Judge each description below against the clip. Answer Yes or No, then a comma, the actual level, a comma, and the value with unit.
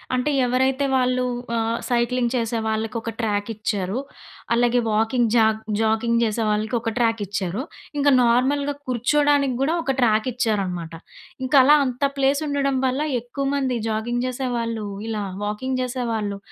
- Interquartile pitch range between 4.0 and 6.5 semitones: No, average, 2.9 semitones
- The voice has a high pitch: Yes, high, 240 Hz